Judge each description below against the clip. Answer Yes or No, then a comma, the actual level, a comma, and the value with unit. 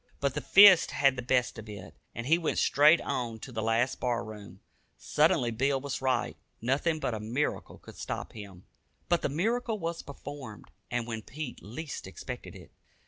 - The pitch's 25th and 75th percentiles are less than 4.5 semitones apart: No, average, 5.3 semitones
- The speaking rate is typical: Yes, average, 185 wpm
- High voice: No, low, 130 Hz